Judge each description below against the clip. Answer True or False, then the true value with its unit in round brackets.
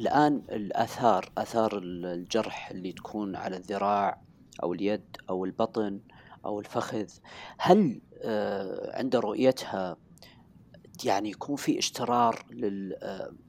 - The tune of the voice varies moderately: True (3.0 semitones)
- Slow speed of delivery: False (95 wpm)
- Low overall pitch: True (105 Hz)